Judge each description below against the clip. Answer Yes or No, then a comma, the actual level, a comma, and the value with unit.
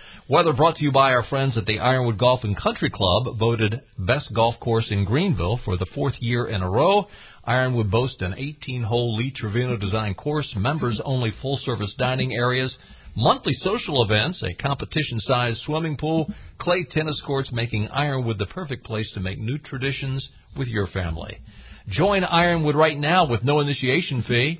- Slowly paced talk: No, average, 180 wpm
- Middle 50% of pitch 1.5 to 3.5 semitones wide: No, average, 4.5 semitones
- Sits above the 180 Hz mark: No, low, 125 Hz